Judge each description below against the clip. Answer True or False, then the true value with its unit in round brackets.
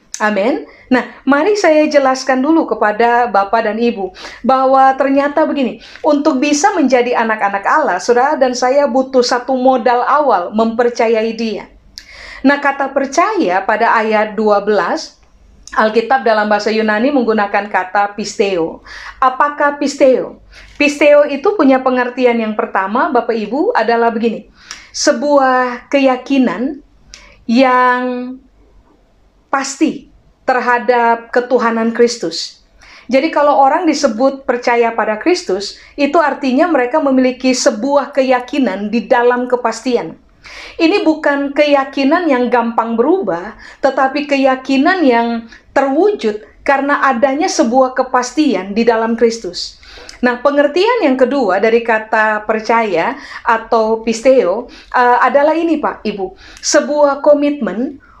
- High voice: True (255 Hz)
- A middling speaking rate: True (110 wpm)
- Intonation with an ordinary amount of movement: True (3.5 semitones)